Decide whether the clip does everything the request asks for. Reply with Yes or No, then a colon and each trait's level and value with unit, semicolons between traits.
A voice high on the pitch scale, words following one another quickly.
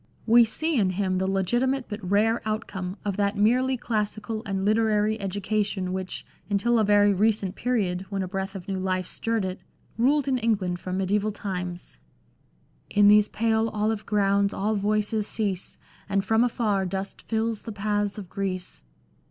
No: high, 205 Hz; average, 170 wpm